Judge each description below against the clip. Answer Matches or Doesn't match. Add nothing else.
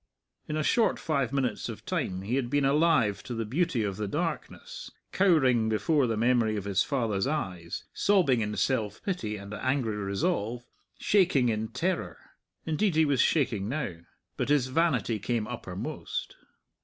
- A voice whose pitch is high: Doesn't match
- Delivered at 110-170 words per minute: Matches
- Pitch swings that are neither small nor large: Doesn't match